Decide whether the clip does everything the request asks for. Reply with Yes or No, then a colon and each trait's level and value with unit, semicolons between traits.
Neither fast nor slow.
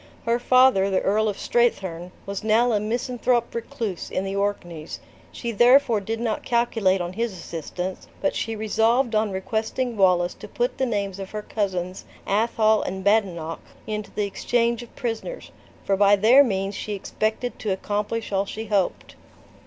Yes: average, 165 wpm